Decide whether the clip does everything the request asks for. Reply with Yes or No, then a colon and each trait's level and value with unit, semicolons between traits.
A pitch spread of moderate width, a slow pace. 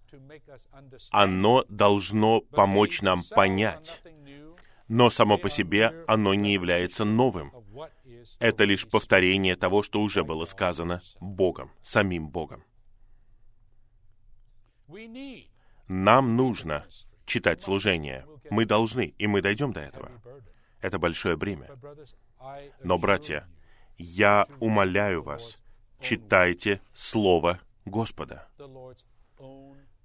Yes: average, 3.9 semitones; slow, 90 wpm